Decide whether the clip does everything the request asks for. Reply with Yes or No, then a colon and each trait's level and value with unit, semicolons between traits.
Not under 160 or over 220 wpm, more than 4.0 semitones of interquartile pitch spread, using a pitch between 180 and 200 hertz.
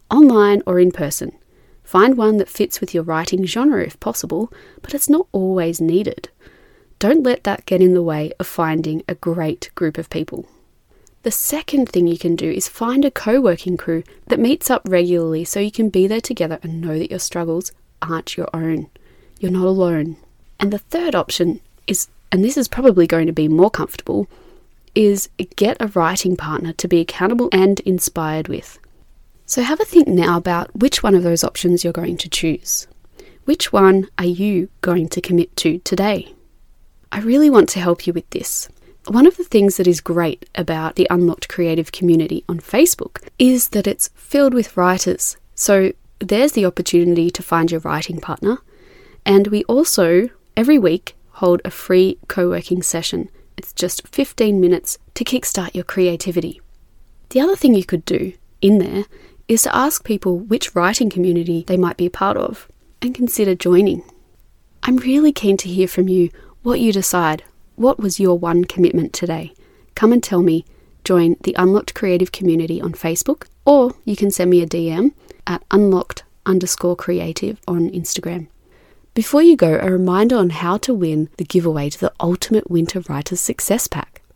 Yes: average, 180 wpm; average, 4.4 semitones; medium, 185 Hz